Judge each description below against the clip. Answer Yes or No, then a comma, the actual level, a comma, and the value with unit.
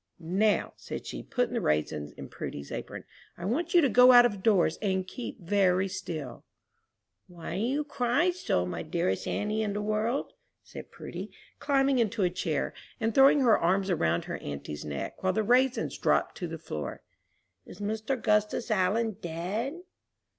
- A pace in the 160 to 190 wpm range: Yes, average, 170 wpm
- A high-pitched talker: Yes, high, 205 Hz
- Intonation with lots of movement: Yes, wide, 5.9 semitones